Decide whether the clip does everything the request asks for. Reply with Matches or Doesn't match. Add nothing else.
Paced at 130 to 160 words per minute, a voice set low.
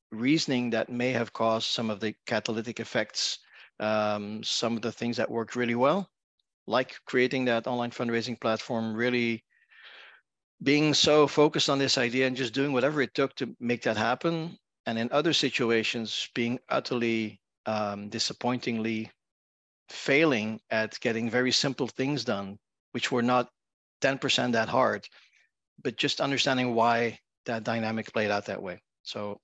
Matches